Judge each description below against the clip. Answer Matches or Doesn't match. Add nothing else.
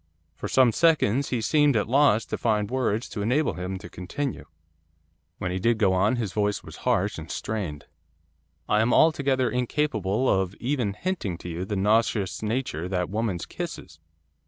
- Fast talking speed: Doesn't match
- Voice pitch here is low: Matches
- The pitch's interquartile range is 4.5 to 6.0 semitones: Matches